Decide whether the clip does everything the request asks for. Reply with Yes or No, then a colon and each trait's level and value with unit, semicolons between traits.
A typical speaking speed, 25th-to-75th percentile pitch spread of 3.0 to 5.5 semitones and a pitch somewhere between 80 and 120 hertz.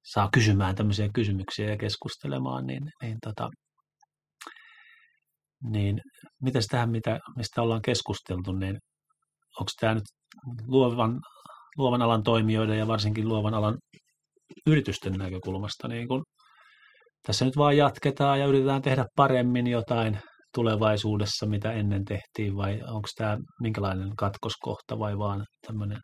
Yes: average, 120 wpm; average, 4.5 semitones; low, 115 Hz